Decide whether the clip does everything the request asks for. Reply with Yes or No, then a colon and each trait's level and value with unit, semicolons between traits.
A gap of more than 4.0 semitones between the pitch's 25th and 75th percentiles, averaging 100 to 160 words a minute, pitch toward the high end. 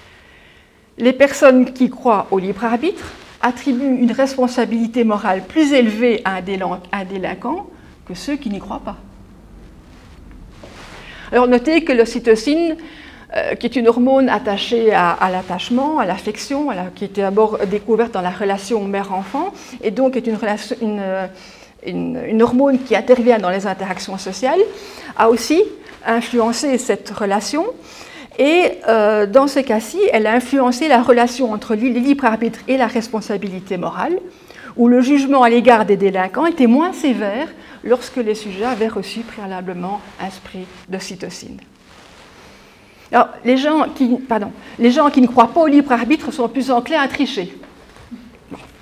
Yes: average, 4.6 semitones; average, 150 wpm; high, 235 Hz